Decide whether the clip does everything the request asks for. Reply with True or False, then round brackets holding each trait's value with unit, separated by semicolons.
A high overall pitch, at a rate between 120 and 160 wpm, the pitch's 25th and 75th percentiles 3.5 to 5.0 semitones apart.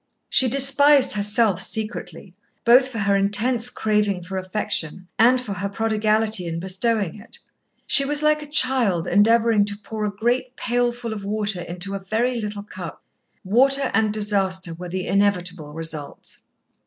True (210 Hz; 155 wpm; 3.8 semitones)